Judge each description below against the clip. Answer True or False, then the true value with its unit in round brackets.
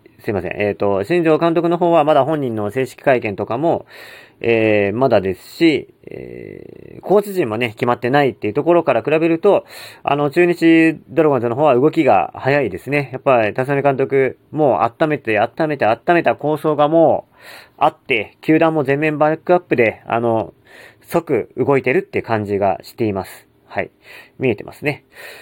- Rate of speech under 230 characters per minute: False (350 characters per minute)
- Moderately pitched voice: True (145 Hz)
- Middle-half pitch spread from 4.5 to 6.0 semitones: True (5.5 semitones)